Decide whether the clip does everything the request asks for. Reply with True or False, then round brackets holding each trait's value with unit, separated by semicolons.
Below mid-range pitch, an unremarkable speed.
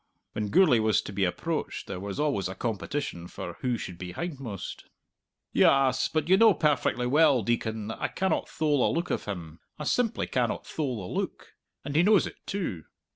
True (125 Hz; 190 wpm)